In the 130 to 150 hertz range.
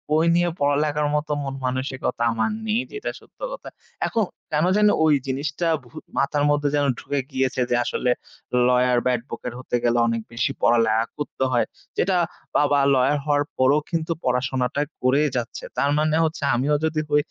Yes: medium, 140 Hz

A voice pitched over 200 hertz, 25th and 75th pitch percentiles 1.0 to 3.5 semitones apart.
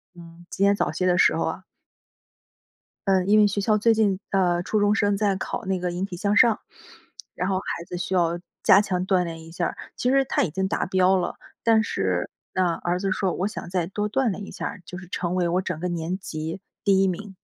No: medium, 185 Hz; narrow, 2.5 semitones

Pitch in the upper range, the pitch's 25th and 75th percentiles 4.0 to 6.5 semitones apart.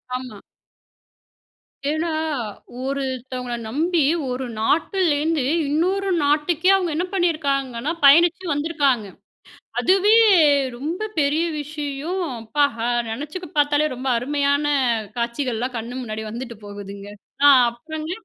Yes: very high, 285 Hz; average, 4.6 semitones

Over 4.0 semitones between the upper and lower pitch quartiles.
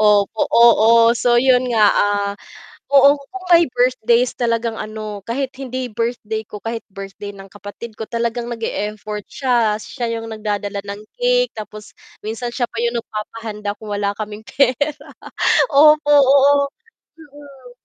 No: average, 3.5 semitones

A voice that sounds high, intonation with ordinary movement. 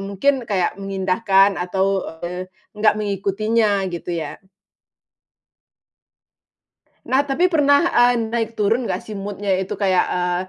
Yes: high, 200 Hz; average, 3.3 semitones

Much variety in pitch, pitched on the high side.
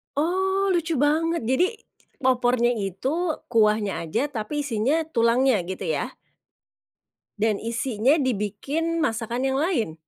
Yes: wide, 6.0 semitones; very high, 255 Hz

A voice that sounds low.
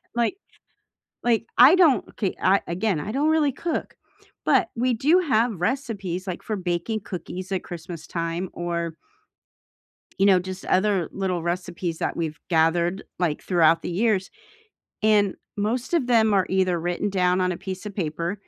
No: high, 190 Hz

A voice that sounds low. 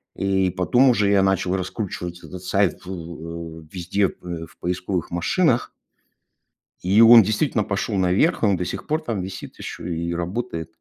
Yes: very low, 95 Hz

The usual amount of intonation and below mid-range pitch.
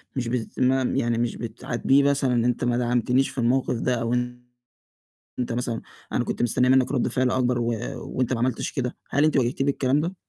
No: narrow, 1.7 semitones; low, 125 Hz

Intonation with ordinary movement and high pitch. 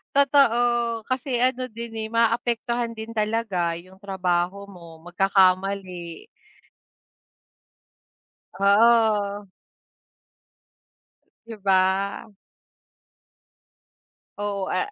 Yes: average, 3.6 semitones; high, 205 Hz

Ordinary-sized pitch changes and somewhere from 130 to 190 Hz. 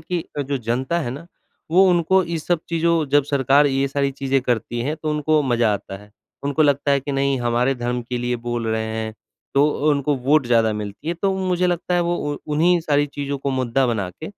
Yes: average, 4.4 semitones; medium, 140 Hz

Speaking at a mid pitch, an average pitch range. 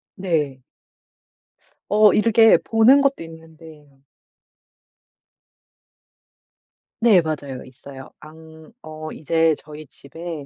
Yes: medium, 160 Hz; average, 4.2 semitones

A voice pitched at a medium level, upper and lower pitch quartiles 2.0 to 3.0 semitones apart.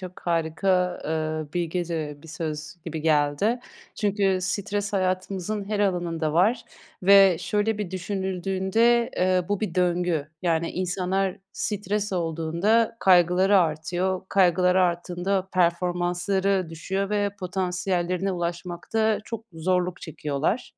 Yes: medium, 180 Hz; narrow, 2.4 semitones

